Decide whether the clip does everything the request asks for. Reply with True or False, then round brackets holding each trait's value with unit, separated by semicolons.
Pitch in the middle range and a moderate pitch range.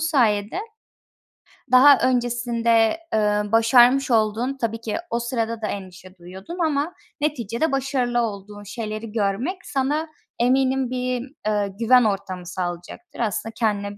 False (230 Hz; 3.8 semitones)